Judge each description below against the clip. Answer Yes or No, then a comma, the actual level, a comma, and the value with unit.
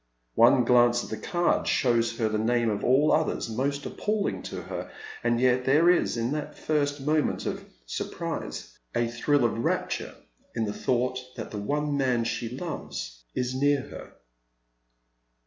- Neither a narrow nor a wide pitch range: Yes, average, 3.7 semitones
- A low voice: Yes, low, 125 Hz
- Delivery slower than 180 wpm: Yes, average, 165 wpm